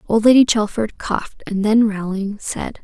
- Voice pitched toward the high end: Yes, high, 215 Hz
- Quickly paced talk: No, average, 170 wpm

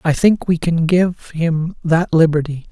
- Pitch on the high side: No, medium, 165 Hz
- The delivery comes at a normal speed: Yes, average, 175 wpm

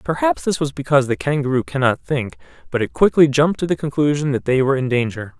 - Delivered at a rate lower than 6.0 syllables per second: No, 6.5 syllables/s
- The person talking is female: No, male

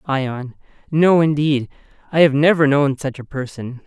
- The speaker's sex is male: Yes, male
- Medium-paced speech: Yes, average, 155 wpm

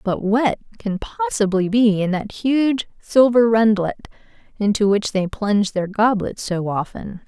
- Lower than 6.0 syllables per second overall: Yes, 4.2 syllables/s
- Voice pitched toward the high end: Yes, high, 205 Hz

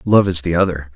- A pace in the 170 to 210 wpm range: No, fast, 250 wpm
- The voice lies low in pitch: Yes, very low, 85 Hz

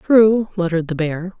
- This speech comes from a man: No, female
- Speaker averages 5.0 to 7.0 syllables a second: Yes, 5.3 syllables/s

